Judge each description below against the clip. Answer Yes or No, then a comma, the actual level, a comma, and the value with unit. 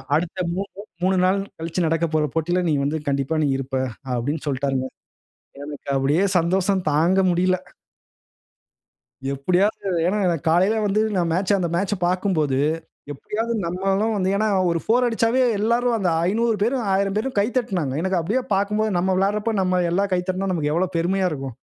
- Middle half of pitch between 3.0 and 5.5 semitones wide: Yes, average, 3.8 semitones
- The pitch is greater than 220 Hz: No, medium, 185 Hz